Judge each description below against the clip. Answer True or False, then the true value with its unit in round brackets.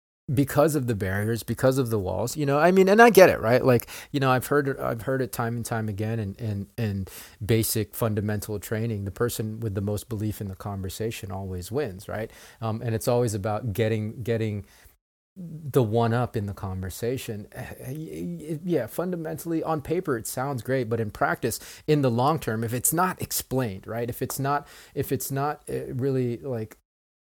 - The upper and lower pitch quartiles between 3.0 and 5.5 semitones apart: True (4.3 semitones)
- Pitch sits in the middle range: False (115 Hz)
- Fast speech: False (190 wpm)